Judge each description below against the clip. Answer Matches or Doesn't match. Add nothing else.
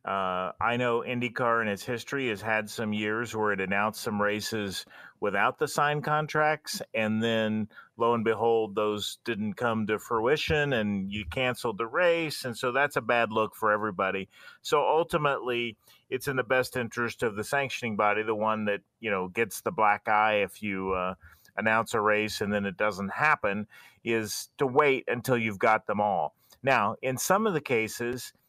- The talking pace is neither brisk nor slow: Matches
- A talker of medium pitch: Doesn't match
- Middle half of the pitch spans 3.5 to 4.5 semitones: Doesn't match